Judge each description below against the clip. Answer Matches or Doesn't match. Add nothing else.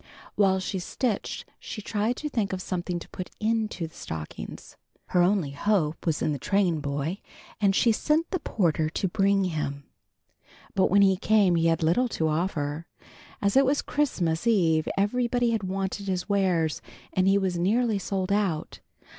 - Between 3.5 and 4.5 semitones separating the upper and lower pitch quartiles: Matches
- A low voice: Doesn't match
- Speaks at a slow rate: Doesn't match